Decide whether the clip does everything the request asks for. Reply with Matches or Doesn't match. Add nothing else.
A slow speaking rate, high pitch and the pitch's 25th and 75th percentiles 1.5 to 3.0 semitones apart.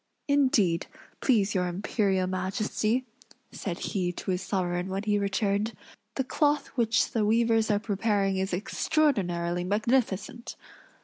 Doesn't match